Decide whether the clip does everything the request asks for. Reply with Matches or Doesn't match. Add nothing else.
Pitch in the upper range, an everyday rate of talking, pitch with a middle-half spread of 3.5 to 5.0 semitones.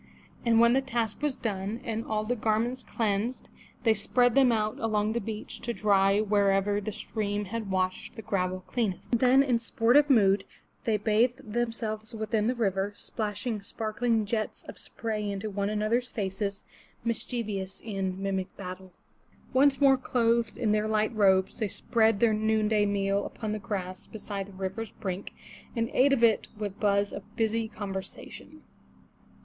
Doesn't match